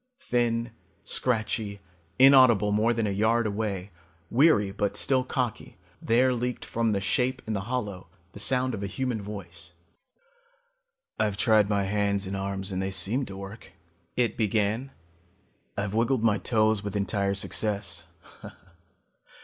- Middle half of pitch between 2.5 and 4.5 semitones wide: Yes, average, 3.2 semitones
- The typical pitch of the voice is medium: No, low, 105 Hz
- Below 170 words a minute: Yes, average, 140 wpm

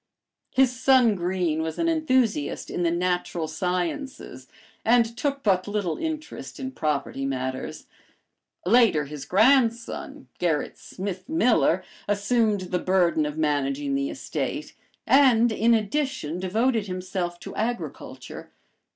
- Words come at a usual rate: No, slow, 120 wpm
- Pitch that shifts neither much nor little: No, wide, 7.1 semitones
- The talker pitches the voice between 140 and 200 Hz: Yes, high, 190 Hz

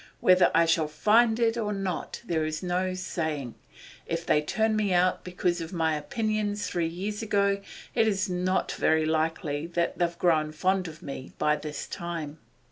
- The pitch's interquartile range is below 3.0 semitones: No, average, 3.9 semitones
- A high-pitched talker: No, medium, 175 Hz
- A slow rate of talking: No, average, 165 wpm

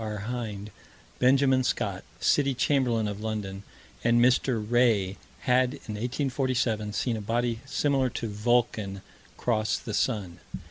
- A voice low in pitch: Yes, low, 115 Hz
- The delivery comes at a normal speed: No, slow, 130 wpm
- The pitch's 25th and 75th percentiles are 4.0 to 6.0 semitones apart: No, average, 3.1 semitones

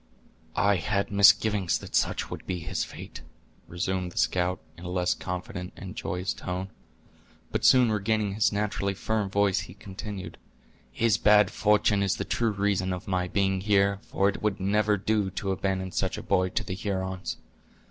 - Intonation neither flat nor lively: No, narrow, 2.0 semitones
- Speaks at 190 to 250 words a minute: No, average, 175 wpm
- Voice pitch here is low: Yes, low, 100 Hz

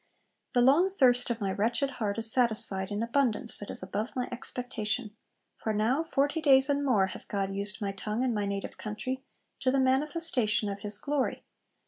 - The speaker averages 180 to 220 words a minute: Yes, average, 185 wpm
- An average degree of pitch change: Yes, average, 4.2 semitones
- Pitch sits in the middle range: No, high, 235 Hz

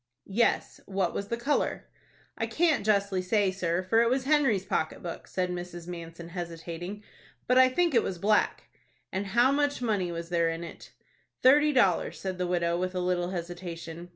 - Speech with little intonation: No, average, 5.0 semitones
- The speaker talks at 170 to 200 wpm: Yes, average, 180 wpm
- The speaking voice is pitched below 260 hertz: Yes, medium, 185 Hz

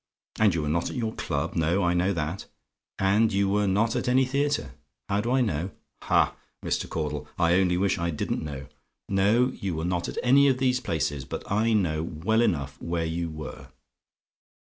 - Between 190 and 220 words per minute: Yes, average, 195 wpm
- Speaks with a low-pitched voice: Yes, very low, 95 Hz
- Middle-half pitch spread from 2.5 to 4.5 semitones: No, wide, 5.5 semitones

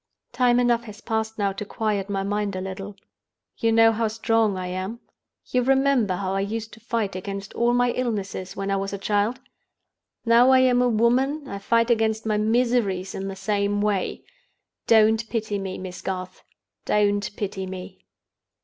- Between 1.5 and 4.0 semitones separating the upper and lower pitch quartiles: Yes, average, 3.0 semitones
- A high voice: Yes, high, 215 Hz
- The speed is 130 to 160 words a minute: No, average, 175 wpm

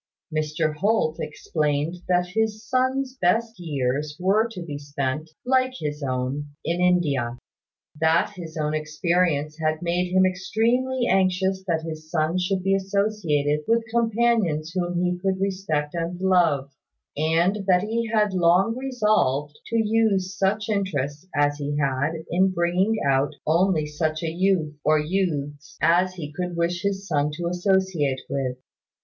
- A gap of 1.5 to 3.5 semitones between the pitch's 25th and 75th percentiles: No, average, 4.3 semitones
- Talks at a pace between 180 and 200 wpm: No, average, 145 wpm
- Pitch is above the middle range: No, medium, 175 Hz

